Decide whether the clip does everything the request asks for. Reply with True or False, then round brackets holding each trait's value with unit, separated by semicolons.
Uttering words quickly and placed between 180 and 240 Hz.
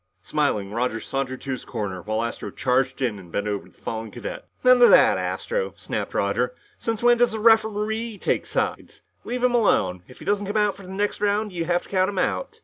True (225 wpm; 185 Hz)